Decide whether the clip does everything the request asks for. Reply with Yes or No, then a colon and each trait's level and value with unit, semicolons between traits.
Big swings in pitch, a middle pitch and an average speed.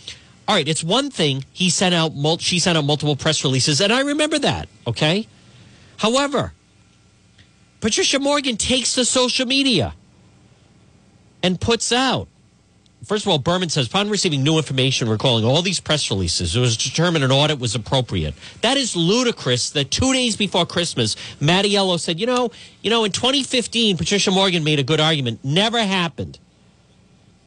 Yes: wide, 8.4 semitones; medium, 175 Hz; average, 160 wpm